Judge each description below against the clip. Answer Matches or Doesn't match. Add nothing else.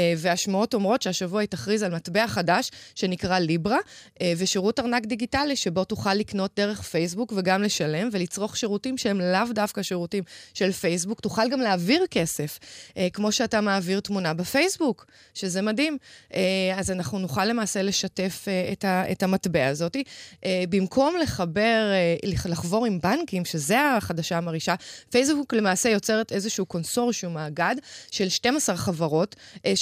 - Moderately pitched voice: Doesn't match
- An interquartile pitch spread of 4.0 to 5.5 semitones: Doesn't match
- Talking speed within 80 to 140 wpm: Matches